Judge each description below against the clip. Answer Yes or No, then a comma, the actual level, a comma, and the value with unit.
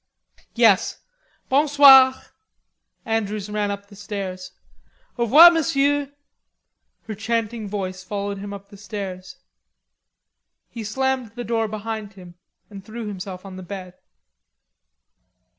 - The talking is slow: Yes, slow, 120 wpm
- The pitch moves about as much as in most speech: Yes, average, 3.1 semitones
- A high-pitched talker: Yes, high, 210 Hz